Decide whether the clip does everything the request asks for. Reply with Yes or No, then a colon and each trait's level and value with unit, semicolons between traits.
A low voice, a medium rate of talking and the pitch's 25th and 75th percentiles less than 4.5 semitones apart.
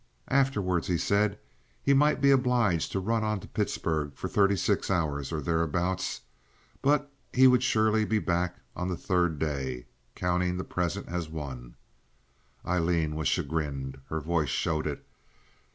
No: very low, 90 Hz; average, 150 wpm; average, 5.3 semitones